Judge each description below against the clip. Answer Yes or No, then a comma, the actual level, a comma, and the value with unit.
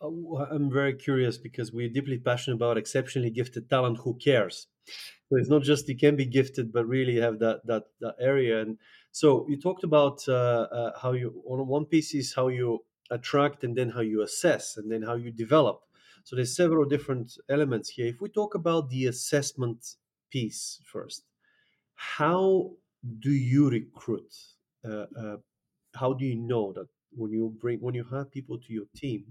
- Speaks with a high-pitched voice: No, low, 130 Hz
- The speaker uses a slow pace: No, average, 180 wpm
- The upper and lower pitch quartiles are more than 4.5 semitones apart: No, average, 3.3 semitones